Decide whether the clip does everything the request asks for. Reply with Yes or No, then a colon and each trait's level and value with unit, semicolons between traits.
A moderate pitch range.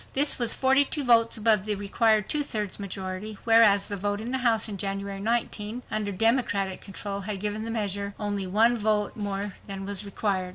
No: narrow, 2.3 semitones